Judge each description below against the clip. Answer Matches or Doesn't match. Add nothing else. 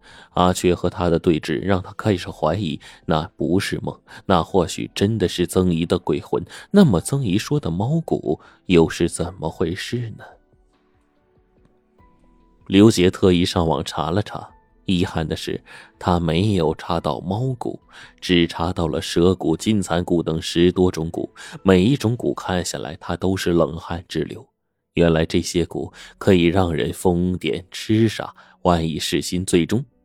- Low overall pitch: Matches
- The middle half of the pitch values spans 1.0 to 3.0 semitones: Matches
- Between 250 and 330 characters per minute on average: Doesn't match